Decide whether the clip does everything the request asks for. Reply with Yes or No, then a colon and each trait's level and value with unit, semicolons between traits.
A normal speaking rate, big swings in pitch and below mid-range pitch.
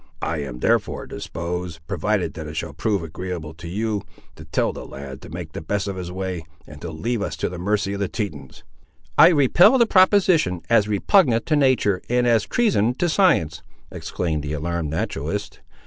Yes: average, 190 wpm; wide, 6.2 semitones; very low, 90 Hz